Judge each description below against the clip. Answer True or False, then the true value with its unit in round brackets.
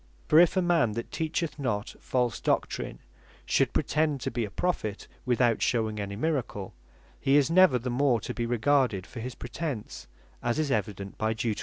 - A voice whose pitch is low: True (125 Hz)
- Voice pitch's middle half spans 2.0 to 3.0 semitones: False (5.1 semitones)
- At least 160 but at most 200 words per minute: True (180 wpm)